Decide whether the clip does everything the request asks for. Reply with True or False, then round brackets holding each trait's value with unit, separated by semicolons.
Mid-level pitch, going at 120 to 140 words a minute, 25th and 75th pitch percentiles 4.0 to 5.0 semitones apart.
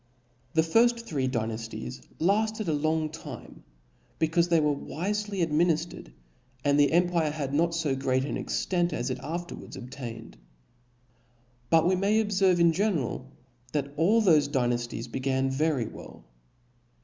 True (155 Hz; 135 wpm; 4.7 semitones)